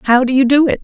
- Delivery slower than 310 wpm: No, fast, 360 wpm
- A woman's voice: Yes, female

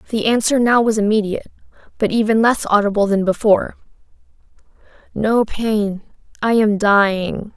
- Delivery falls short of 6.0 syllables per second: Yes, 5.1 syllables/s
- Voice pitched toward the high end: Yes, high, 215 Hz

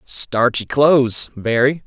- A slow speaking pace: Yes, slow, 95 wpm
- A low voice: Yes, low, 125 Hz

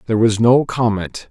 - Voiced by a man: Yes, male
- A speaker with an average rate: Yes, average, 185 wpm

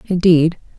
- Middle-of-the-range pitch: Yes, medium, 170 Hz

